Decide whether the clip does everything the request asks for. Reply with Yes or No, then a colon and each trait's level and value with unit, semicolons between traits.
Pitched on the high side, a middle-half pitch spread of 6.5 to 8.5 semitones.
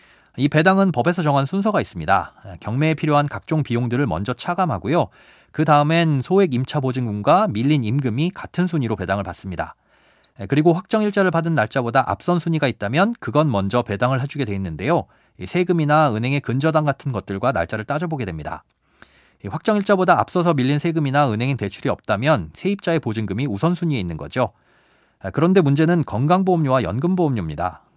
No: medium, 145 Hz; wide, 6.8 semitones